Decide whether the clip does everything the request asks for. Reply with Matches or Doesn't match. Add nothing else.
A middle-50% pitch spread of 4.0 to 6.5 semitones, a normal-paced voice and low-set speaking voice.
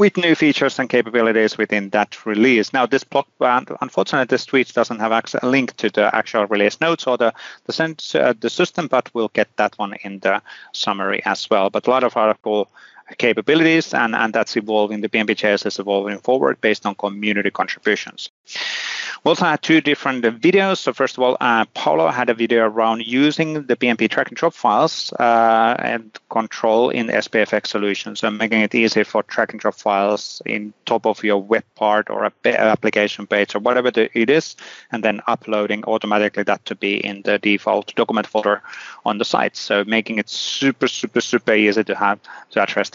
Doesn't match